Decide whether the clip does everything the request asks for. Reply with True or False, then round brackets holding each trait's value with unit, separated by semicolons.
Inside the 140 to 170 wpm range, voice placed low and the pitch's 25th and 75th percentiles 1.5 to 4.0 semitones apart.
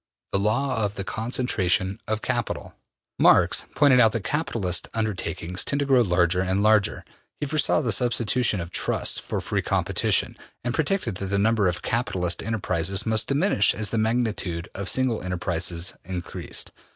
False (160 wpm; 110 Hz; 4.8 semitones)